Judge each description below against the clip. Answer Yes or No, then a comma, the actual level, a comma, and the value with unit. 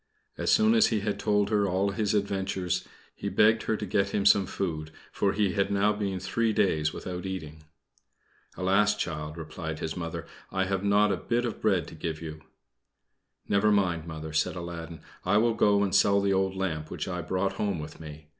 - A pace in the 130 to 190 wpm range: No, average, 200 wpm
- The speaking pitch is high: No, very low, 95 Hz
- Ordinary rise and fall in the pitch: Yes, average, 3.7 semitones